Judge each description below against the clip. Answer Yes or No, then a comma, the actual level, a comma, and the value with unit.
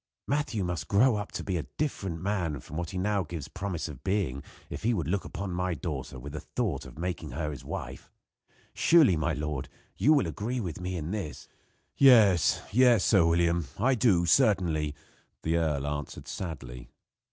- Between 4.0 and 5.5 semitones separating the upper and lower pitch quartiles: Yes, average, 4.9 semitones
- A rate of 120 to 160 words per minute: No, average, 185 wpm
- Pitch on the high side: No, very low, 85 Hz